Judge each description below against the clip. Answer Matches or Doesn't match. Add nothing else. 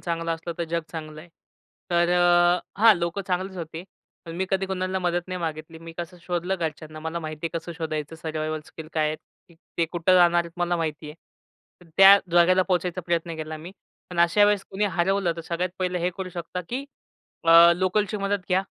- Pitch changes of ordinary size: Doesn't match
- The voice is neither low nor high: Matches